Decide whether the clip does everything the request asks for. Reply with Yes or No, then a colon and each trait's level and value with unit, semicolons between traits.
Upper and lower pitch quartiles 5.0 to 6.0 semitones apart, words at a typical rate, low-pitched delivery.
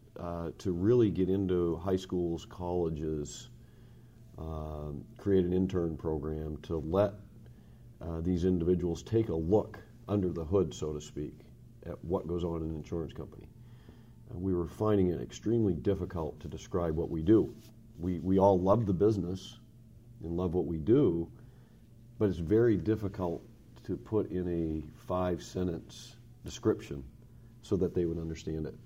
Yes: average, 5.3 semitones; average, 155 wpm; very low, 90 Hz